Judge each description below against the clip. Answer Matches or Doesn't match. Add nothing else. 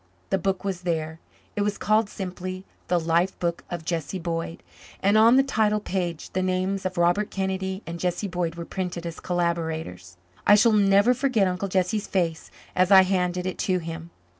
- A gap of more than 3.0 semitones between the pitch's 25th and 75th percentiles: Doesn't match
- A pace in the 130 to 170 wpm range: Doesn't match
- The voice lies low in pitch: Doesn't match